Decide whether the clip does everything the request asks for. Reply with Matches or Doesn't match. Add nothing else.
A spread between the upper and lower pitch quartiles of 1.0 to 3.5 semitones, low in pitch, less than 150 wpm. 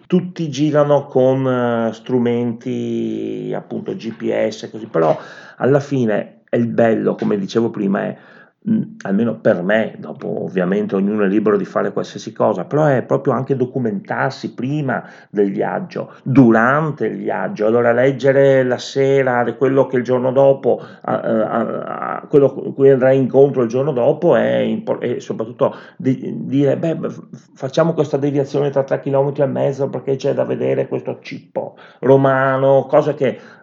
Matches